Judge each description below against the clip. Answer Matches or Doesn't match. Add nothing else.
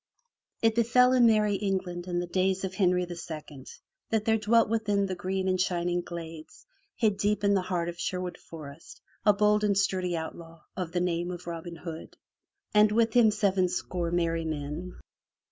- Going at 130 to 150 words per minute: Doesn't match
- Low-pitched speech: Doesn't match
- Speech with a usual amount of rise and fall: Matches